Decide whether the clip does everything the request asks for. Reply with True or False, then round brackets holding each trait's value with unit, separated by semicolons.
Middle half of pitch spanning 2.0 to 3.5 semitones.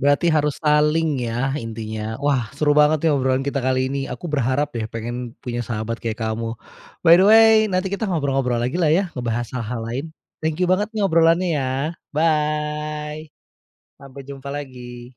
False (4.1 semitones)